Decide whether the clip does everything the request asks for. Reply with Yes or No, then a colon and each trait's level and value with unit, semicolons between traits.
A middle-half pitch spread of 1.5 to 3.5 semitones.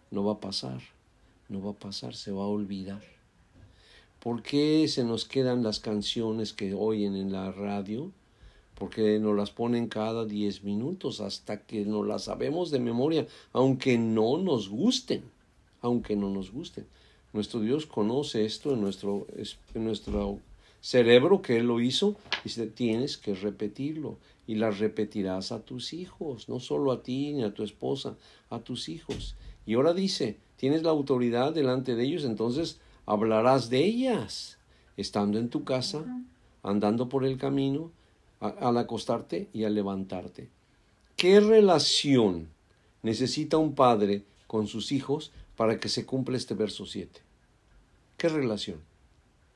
No: average, 4.1 semitones